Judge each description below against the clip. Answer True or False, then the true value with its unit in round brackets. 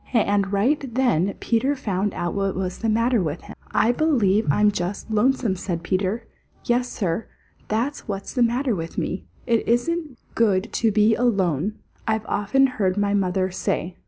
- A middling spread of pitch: True (4.1 semitones)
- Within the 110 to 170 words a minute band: True (165 wpm)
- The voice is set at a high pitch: True (210 Hz)